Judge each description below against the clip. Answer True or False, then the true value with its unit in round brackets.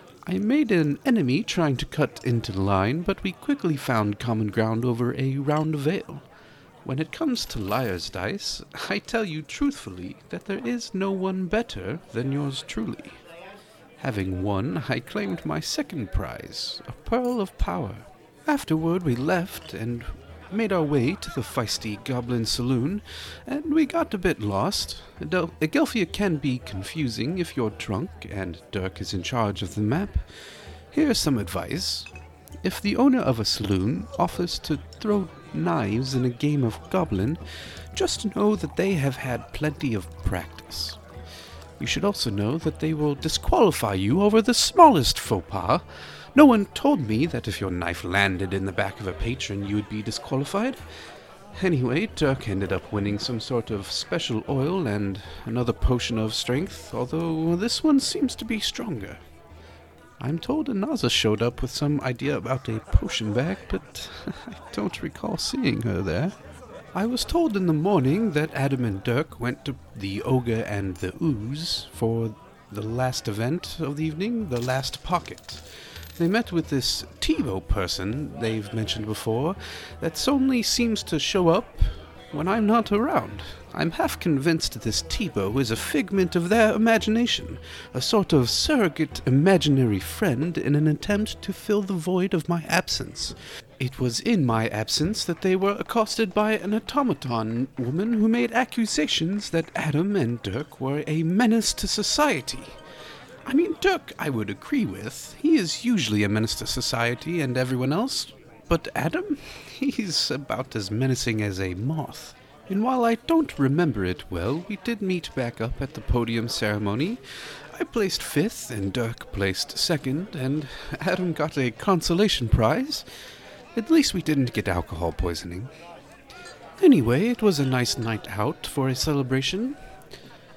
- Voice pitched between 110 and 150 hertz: True (140 Hz)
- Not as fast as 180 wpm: True (165 wpm)